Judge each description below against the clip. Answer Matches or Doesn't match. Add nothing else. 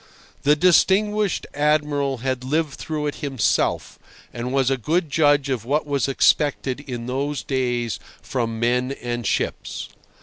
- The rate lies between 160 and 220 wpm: Doesn't match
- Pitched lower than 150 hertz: Matches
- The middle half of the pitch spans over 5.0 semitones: Doesn't match